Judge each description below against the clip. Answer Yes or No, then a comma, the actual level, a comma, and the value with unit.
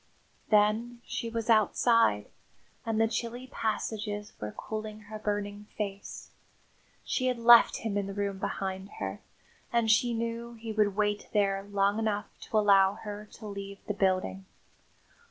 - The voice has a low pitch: No, high, 210 Hz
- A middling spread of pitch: No, narrow, 2.1 semitones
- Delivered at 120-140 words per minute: No, average, 150 wpm